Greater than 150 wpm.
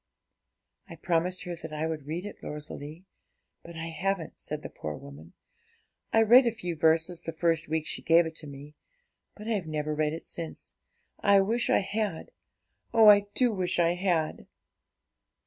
Yes: average, 175 wpm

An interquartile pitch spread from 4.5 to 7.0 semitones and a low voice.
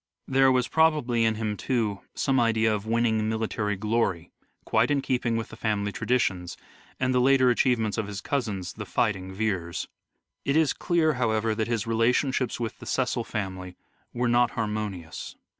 No: average, 3.0 semitones; low, 115 Hz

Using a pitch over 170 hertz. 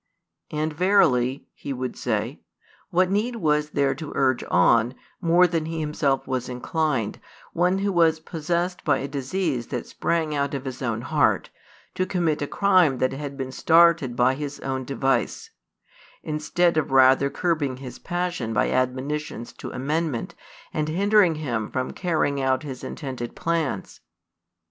No: medium, 145 Hz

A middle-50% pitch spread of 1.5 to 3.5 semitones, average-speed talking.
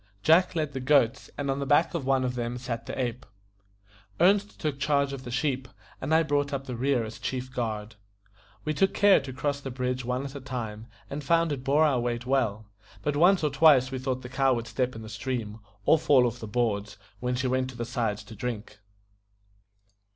No: average, 2.9 semitones; fast, 220 wpm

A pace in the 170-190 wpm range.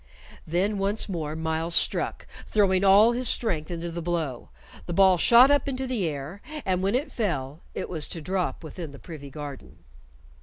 Yes: average, 180 wpm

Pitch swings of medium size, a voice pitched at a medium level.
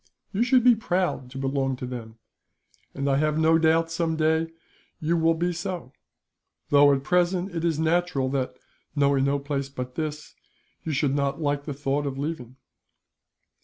Yes: average, 3.2 semitones; medium, 150 Hz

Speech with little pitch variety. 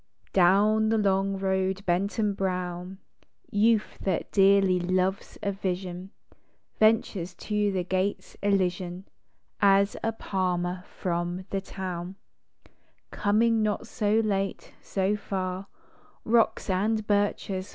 Yes: narrow, 1.9 semitones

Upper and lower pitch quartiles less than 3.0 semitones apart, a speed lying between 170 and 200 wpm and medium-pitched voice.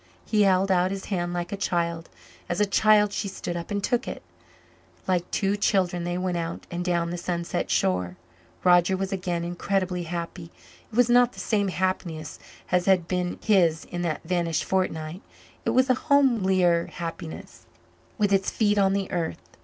Yes: narrow, 2.4 semitones; average, 175 wpm; medium, 180 Hz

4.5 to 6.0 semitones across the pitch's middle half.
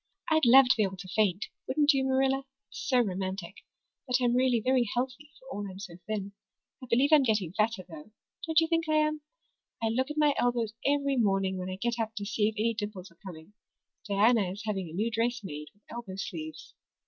Yes: average, 5.1 semitones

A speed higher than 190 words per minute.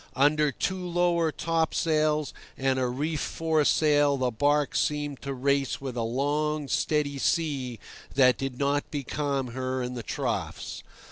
No: average, 140 wpm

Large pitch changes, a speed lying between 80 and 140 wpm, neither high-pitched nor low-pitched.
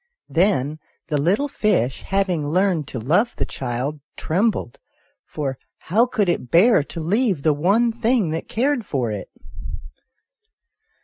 Yes: wide, 6.9 semitones; slow, 135 wpm; medium, 170 Hz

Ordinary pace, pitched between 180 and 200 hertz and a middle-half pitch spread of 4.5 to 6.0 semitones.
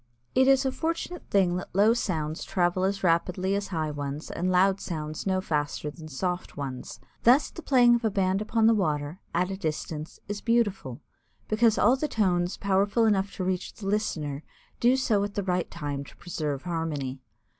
Yes: average, 190 wpm; medium, 185 Hz; average, 5.2 semitones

